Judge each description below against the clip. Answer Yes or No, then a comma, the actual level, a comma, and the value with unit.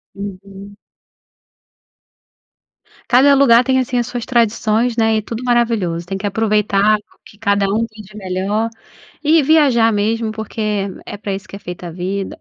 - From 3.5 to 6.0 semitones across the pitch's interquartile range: No, average, 3.0 semitones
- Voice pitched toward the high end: Yes, high, 215 Hz